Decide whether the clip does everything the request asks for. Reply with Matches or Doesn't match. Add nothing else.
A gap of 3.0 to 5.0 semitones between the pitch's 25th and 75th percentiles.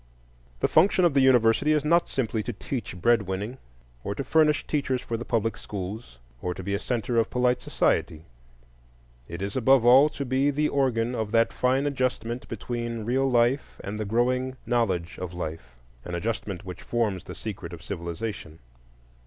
Matches